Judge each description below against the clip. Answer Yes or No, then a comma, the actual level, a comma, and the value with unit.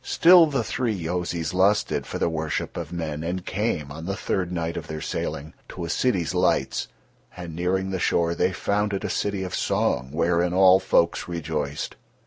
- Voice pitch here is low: Yes, very low, 90 Hz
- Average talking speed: Yes, average, 185 wpm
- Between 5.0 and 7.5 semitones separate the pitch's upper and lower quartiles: No, average, 2.7 semitones